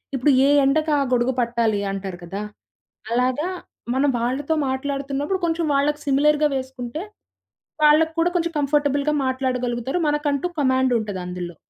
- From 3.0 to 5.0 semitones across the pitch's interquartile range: Yes, average, 3.4 semitones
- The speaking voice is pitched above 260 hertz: Yes, very high, 270 Hz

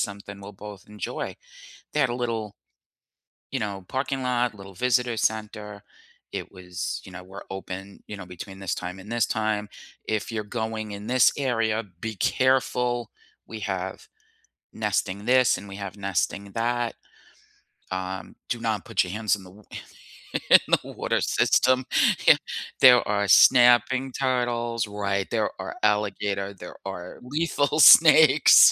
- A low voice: Yes, low, 105 Hz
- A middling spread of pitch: Yes, average, 3.7 semitones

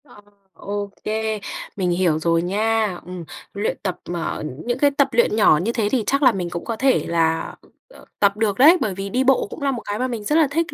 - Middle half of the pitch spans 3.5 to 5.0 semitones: No, wide, 5.5 semitones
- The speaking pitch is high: Yes, high, 215 Hz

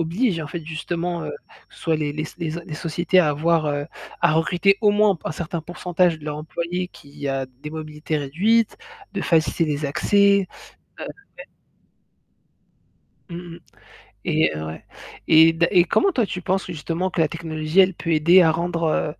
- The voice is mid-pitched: Yes, medium, 165 Hz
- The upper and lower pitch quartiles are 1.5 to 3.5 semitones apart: Yes, average, 2.8 semitones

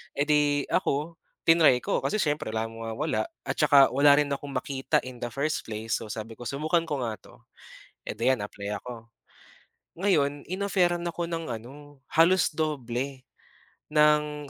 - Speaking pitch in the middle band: Yes, medium, 145 Hz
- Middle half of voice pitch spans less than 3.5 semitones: No, average, 4.4 semitones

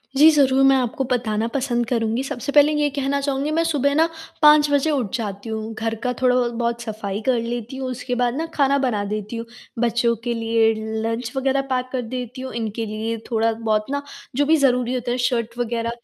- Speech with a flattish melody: No, average, 3.1 semitones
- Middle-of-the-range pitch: No, high, 245 Hz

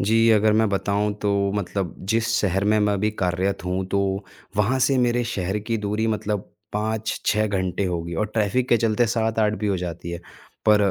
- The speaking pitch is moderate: No, low, 105 Hz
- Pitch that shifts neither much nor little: No, narrow, 2.3 semitones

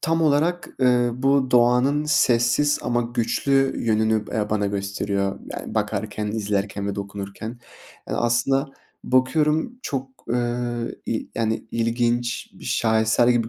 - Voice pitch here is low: Yes, low, 120 Hz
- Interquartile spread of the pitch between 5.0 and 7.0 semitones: No, average, 3.3 semitones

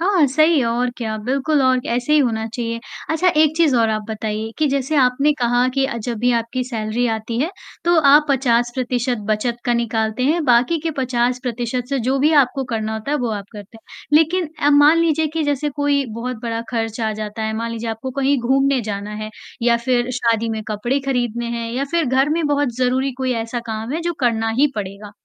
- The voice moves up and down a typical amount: Yes, average, 3.6 semitones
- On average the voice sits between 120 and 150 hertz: No, very high, 250 Hz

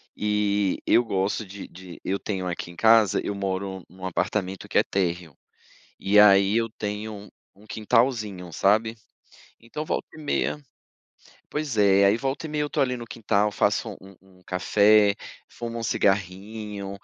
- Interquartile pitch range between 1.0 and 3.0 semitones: Yes, average, 2.7 semitones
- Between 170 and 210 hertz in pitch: No, low, 100 Hz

